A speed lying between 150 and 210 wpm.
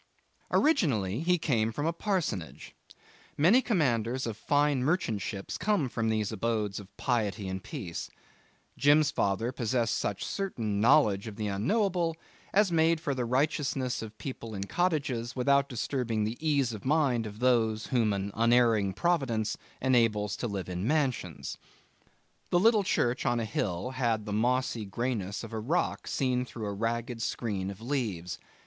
Yes: average, 155 wpm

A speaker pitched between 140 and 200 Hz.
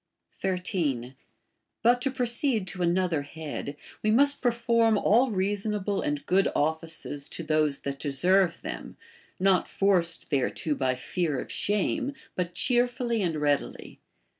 Yes: medium, 185 Hz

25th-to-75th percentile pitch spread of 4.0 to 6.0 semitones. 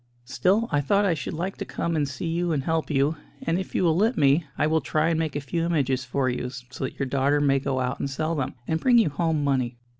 No: average, 3.6 semitones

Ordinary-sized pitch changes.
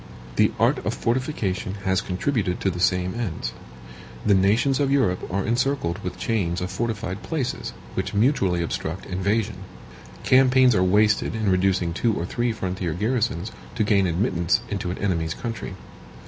Yes: average, 4.3 semitones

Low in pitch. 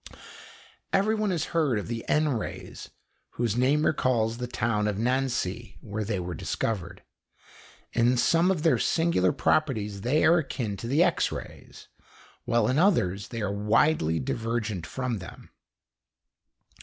Yes: low, 120 Hz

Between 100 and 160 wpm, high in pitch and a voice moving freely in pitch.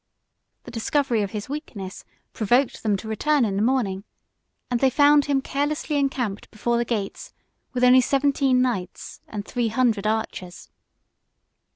No: average, 150 wpm; high, 240 Hz; average, 4.5 semitones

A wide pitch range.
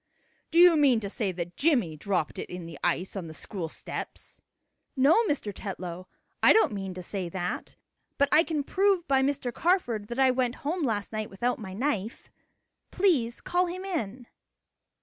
Yes: wide, 7.6 semitones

